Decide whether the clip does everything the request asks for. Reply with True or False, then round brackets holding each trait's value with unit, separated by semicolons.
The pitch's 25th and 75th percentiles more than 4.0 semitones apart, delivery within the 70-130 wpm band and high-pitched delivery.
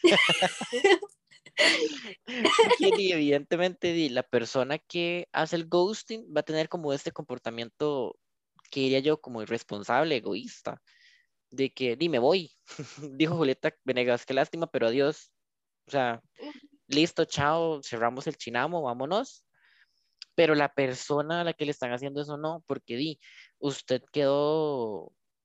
False (4.5 semitones; 125 wpm; 155 Hz)